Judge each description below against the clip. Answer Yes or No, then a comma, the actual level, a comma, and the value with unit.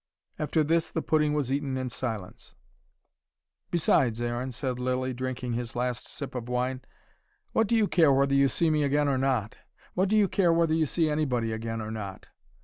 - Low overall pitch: Yes, low, 130 Hz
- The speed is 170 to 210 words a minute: Yes, average, 190 wpm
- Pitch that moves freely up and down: No, average, 4.1 semitones